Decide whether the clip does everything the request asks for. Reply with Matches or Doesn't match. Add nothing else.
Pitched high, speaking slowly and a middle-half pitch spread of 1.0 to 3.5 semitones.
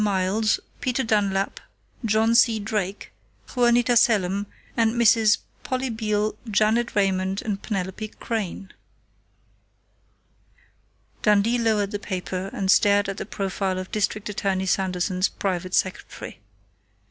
Matches